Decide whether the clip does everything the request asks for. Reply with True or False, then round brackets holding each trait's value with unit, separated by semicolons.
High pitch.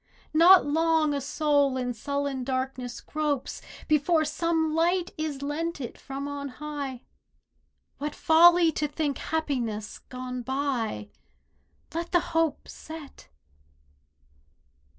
True (290 Hz)